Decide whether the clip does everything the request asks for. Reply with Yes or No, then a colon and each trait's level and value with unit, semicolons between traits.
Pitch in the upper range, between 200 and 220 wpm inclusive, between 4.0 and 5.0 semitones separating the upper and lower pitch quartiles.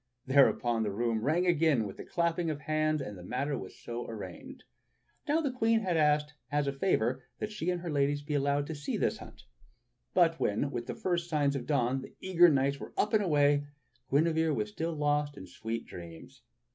No: medium, 145 Hz; fast, 205 wpm; average, 4.6 semitones